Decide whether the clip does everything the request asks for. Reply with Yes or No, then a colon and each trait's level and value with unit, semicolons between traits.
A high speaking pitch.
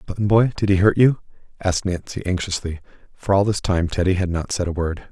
No: very low, 95 Hz